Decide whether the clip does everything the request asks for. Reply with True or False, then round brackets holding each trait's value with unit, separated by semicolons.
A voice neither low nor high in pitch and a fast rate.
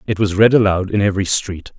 False (100 Hz; 235 wpm)